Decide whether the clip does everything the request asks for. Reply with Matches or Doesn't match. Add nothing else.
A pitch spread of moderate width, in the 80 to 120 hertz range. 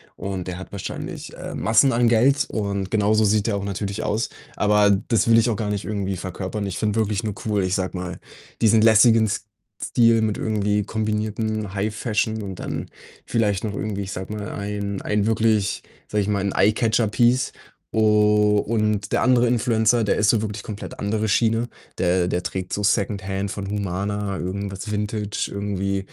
Doesn't match